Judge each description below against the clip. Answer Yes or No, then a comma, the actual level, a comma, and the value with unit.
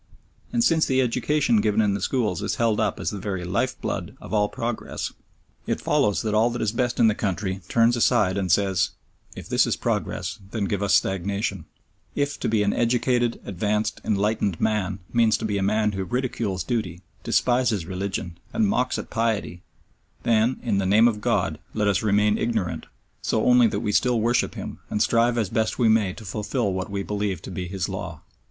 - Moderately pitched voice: No, low, 105 Hz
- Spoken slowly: No, average, 200 wpm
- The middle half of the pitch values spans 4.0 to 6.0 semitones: No, average, 3.1 semitones